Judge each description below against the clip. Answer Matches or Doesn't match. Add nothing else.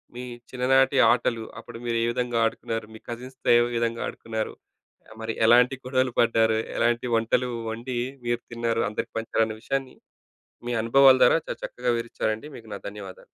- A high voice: Doesn't match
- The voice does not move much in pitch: Matches